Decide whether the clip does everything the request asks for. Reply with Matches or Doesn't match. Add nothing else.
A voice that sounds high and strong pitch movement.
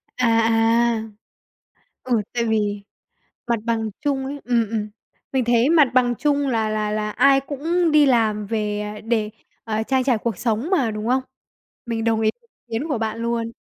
Doesn't match